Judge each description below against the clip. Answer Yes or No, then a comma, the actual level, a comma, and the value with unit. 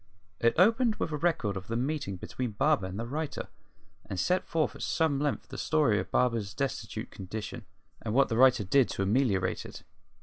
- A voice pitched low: Yes, low, 125 Hz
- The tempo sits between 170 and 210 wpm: Yes, average, 195 wpm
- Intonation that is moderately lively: No, wide, 6.4 semitones